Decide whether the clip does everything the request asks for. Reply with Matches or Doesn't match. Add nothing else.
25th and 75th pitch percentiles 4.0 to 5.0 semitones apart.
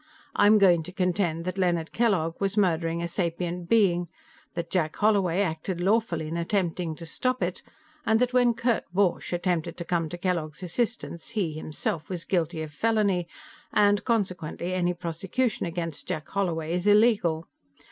Doesn't match